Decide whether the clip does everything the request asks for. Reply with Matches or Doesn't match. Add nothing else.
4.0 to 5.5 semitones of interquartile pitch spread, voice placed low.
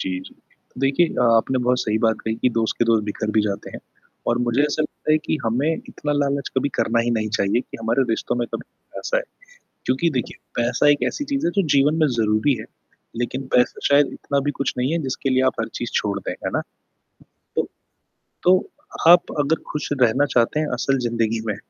Matches